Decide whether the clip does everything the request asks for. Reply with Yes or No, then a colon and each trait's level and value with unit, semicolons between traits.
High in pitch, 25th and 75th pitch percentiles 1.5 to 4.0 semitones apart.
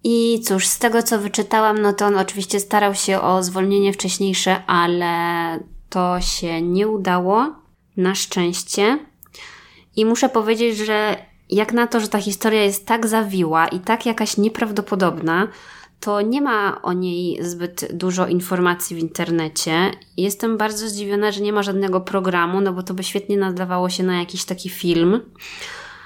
Yes: high, 195 Hz; average, 2.9 semitones